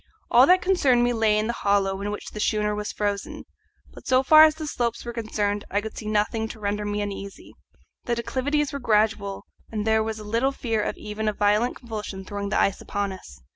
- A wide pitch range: No, narrow, 2.6 semitones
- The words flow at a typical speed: No, fast, 215 wpm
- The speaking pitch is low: No, high, 215 Hz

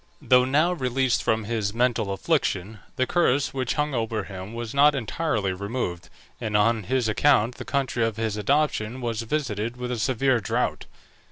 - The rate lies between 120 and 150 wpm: No, average, 170 wpm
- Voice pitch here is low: Yes, low, 120 Hz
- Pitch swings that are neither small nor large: Yes, average, 3.6 semitones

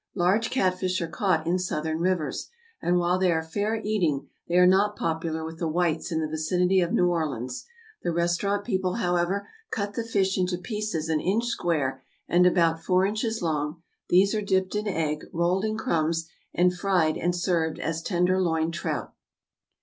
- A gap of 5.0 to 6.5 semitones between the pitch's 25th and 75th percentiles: No, average, 2.9 semitones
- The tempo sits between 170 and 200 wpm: Yes, average, 180 wpm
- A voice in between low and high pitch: Yes, medium, 180 Hz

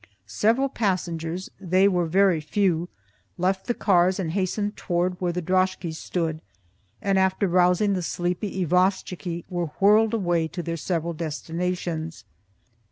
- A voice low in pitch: No, medium, 180 Hz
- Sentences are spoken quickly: No, slow, 135 wpm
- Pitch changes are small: Yes, narrow, 2.1 semitones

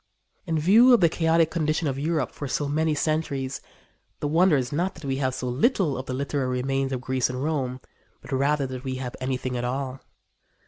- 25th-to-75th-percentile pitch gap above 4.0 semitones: No, average, 3.4 semitones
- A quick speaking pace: Yes, fast, 210 wpm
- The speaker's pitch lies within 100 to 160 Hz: Yes, medium, 140 Hz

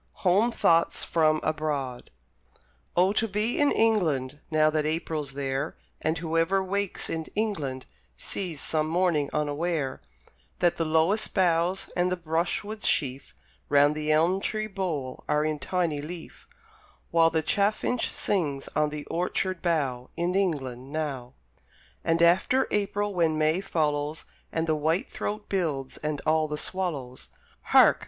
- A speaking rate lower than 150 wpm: Yes, average, 140 wpm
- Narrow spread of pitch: No, average, 3.7 semitones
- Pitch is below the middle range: No, medium, 160 Hz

